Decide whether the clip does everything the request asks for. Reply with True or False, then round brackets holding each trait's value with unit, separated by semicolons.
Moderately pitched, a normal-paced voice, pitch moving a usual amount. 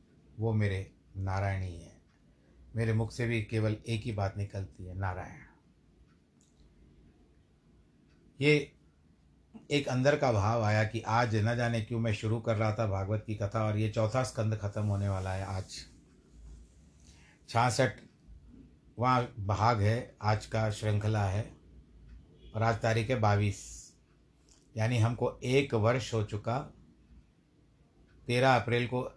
False (105 Hz; 135 wpm; 4.7 semitones)